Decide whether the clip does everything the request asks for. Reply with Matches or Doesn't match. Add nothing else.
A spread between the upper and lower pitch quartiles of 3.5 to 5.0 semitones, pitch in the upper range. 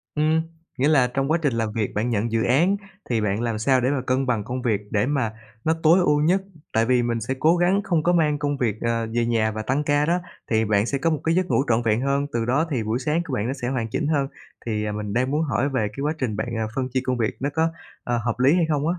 Doesn't match